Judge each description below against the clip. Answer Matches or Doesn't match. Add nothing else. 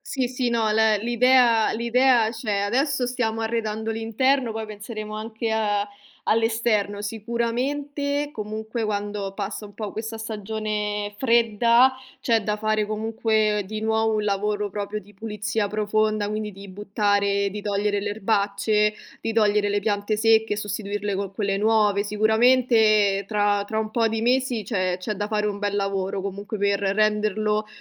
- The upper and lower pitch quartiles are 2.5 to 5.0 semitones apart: Doesn't match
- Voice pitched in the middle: Doesn't match